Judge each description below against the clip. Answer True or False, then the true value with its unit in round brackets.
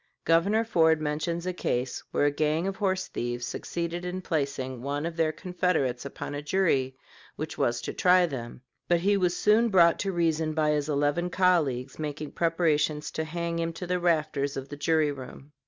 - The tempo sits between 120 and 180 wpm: False (190 wpm)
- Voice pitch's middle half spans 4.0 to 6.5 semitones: False (3.5 semitones)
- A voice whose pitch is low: False (160 Hz)